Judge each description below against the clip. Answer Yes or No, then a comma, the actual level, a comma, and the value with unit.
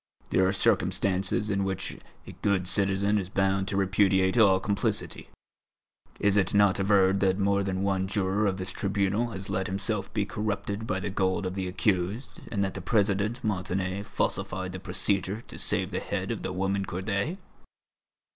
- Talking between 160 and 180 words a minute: Yes, average, 175 wpm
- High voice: No, very low, 95 Hz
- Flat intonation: Yes, narrow, 1.2 semitones